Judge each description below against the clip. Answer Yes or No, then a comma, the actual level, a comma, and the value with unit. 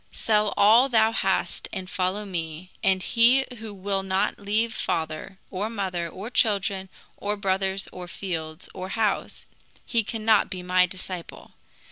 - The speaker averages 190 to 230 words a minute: No, average, 145 wpm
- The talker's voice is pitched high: Yes, high, 195 Hz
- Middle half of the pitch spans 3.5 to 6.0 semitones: No, narrow, 2.6 semitones